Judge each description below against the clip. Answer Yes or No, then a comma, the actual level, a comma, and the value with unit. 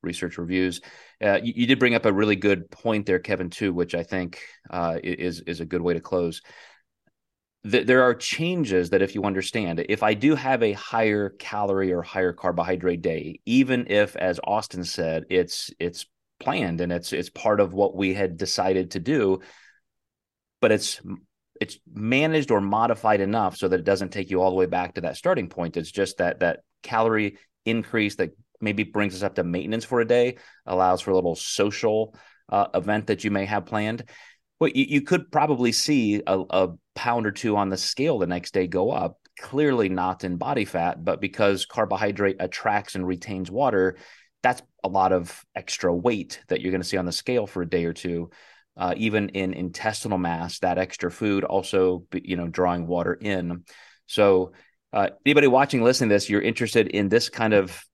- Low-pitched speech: Yes, very low, 95 Hz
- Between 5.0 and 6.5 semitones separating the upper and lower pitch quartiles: No, average, 3.3 semitones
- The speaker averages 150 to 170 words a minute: No, average, 195 wpm